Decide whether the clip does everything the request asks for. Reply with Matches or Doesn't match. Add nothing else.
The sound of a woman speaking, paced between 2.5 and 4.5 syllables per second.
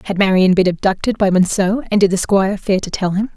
Doesn't match